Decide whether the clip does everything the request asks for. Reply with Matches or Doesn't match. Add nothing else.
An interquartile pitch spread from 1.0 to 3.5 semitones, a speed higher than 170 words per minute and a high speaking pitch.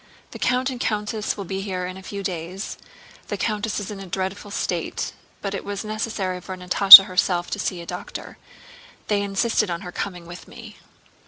Matches